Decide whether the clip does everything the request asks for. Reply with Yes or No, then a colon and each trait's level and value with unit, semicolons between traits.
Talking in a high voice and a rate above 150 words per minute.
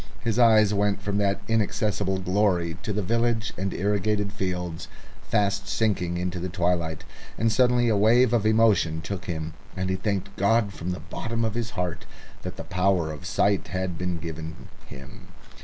No: low, 100 Hz; average, 175 wpm